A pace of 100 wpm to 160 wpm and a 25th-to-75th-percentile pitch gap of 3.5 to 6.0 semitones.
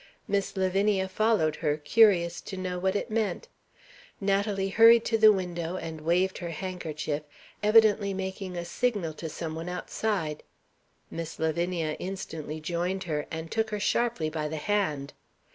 Yes: average, 150 wpm; average, 4.0 semitones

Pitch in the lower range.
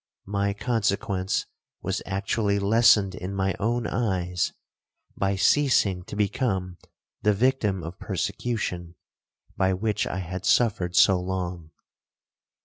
Yes: low, 100 Hz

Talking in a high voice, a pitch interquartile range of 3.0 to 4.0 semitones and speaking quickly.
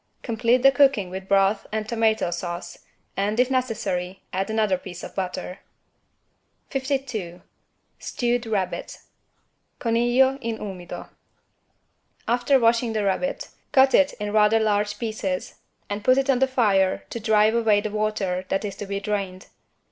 No: high, 215 Hz; average, 3.7 semitones; average, 145 wpm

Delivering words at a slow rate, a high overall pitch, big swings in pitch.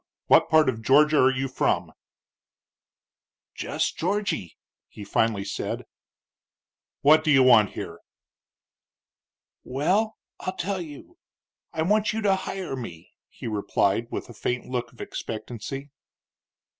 No: slow, 125 wpm; low, 135 Hz; wide, 6.9 semitones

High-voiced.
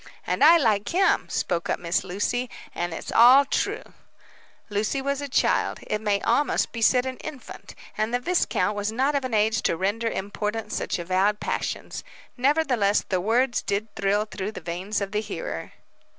Yes: high, 215 Hz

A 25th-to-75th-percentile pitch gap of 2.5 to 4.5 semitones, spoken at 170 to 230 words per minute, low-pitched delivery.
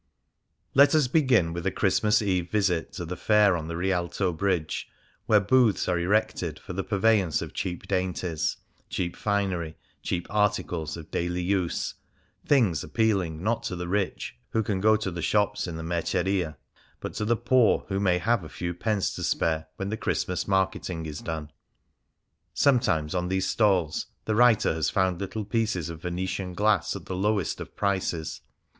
Yes: average, 3.5 semitones; average, 180 wpm; very low, 95 Hz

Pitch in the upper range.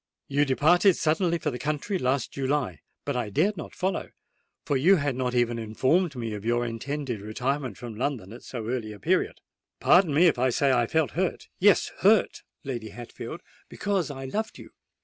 No: low, 135 Hz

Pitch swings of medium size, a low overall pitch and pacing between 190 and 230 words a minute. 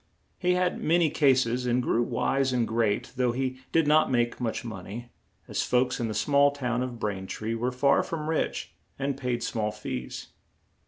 Yes: average, 3.1 semitones; low, 125 Hz; average, 200 wpm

